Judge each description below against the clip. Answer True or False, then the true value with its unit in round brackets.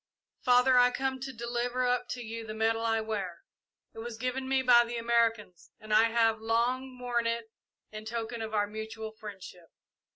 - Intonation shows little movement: True (2.1 semitones)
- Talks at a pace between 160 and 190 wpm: True (185 wpm)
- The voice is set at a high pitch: True (230 Hz)